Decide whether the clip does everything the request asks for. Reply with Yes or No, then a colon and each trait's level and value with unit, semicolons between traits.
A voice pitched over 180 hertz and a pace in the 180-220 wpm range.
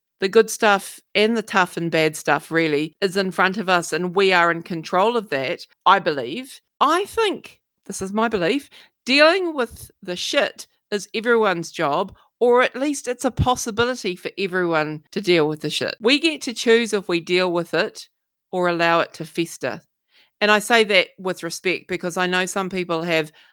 Yes: high, 190 Hz; average, 195 wpm